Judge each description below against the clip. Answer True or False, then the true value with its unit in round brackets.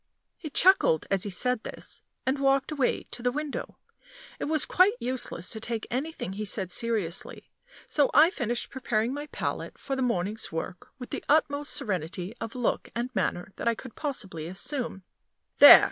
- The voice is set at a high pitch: True (240 Hz)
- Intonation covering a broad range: True (6.1 semitones)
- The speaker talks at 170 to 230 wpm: True (175 wpm)